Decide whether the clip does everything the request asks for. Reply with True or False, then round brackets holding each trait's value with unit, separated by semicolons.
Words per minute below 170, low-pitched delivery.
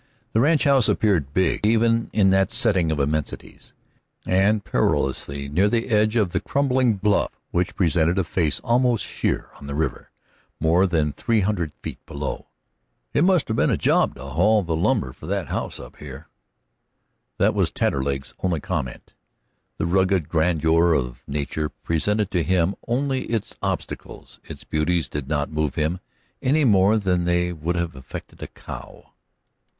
True (160 wpm; 90 Hz)